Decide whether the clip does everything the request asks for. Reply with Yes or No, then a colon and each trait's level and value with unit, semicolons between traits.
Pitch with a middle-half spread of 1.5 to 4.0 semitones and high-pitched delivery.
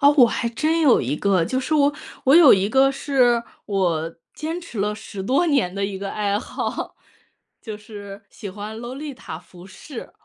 No: wide, 5.6 semitones; high, 220 Hz